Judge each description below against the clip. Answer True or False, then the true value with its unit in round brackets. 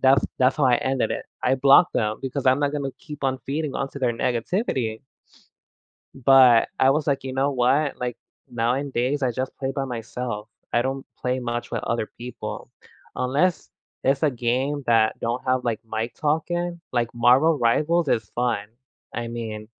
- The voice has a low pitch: True (130 Hz)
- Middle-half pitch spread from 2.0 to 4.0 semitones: True (2.8 semitones)